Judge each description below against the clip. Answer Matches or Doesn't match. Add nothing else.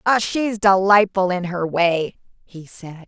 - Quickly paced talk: Doesn't match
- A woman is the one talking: Matches